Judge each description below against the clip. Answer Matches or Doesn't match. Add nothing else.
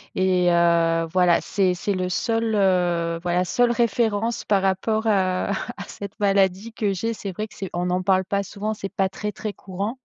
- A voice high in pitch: Matches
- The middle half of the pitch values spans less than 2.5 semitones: Doesn't match